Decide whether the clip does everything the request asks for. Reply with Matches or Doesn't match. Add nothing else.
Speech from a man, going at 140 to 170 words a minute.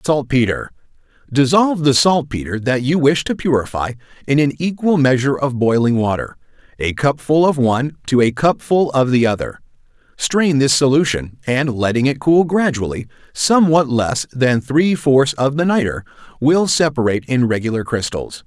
Matches